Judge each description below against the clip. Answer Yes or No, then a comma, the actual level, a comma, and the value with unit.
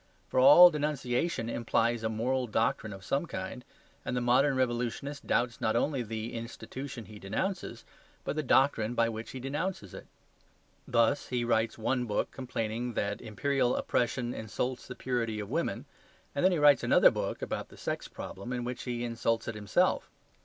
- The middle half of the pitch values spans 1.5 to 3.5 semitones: Yes, average, 2.8 semitones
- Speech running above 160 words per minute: Yes, average, 175 wpm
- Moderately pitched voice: No, low, 120 Hz